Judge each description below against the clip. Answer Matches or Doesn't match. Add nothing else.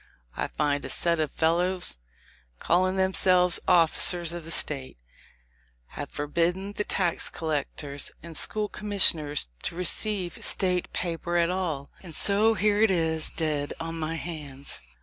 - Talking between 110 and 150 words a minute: Matches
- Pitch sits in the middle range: Matches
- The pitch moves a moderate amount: Matches